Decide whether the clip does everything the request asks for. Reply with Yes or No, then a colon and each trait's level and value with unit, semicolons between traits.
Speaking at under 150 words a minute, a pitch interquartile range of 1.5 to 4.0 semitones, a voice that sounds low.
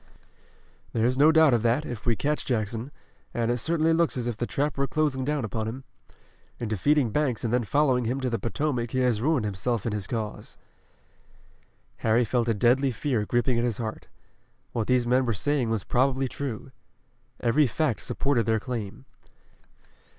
No: average, 180 wpm; average, 3.3 semitones; low, 120 Hz